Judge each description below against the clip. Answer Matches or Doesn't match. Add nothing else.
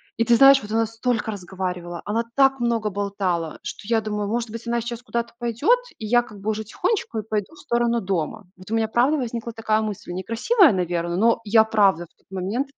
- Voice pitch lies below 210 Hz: Doesn't match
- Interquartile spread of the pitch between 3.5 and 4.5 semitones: Doesn't match